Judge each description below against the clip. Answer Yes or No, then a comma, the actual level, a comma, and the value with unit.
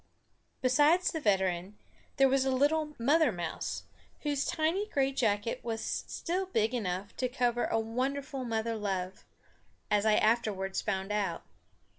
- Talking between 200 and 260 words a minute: No, average, 140 wpm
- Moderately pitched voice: No, high, 235 Hz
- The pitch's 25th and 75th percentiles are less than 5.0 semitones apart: No, average, 5.3 semitones